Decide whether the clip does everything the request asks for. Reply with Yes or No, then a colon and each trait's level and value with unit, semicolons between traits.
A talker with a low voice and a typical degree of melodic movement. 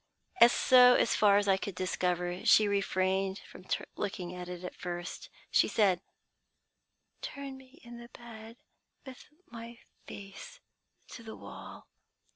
No: high, 200 Hz; average, 4.3 semitones